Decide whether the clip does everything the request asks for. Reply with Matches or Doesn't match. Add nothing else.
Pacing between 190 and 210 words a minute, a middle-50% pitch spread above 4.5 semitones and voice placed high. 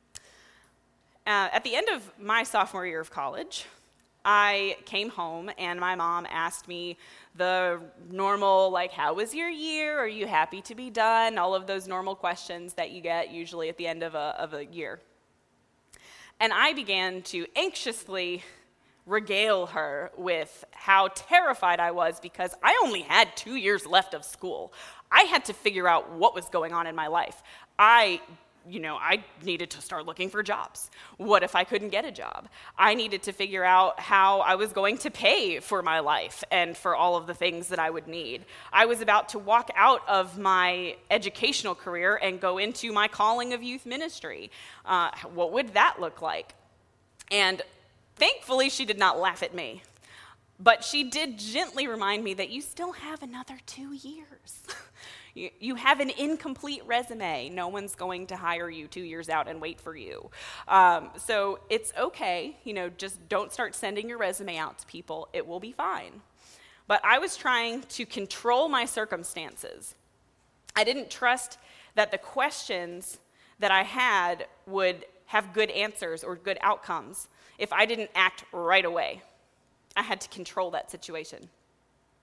Doesn't match